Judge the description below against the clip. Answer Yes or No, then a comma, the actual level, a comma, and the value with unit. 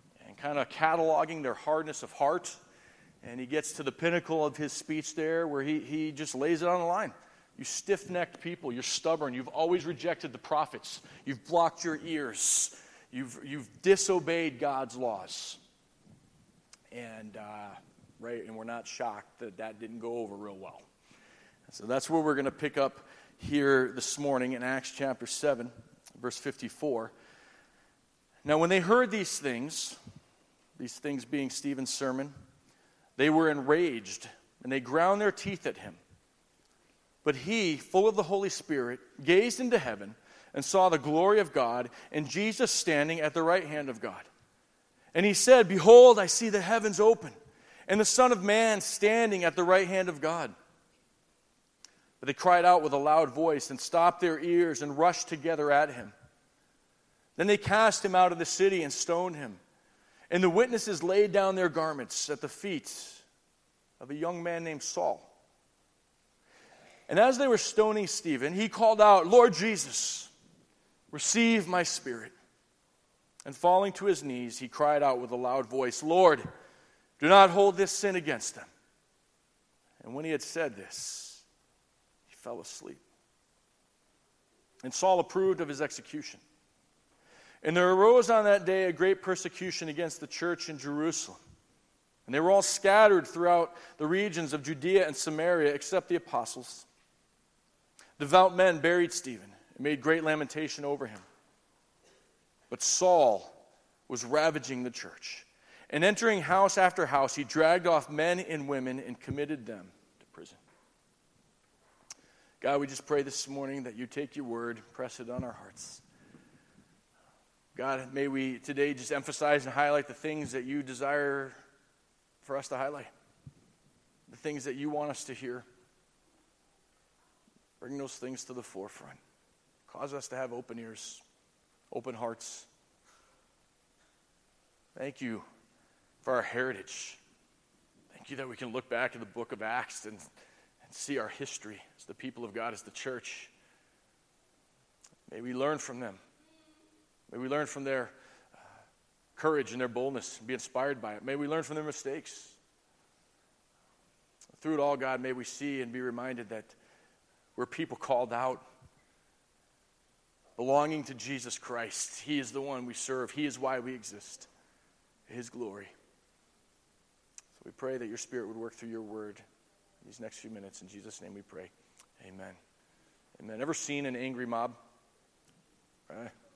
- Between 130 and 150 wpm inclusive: No, average, 160 wpm